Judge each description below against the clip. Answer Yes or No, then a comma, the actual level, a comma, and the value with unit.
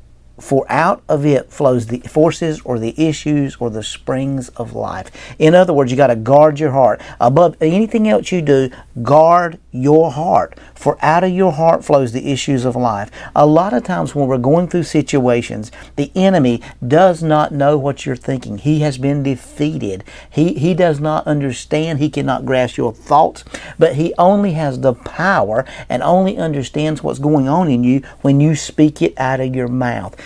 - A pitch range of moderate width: Yes, average, 3.7 semitones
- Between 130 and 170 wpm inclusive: No, average, 185 wpm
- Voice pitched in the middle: Yes, medium, 145 Hz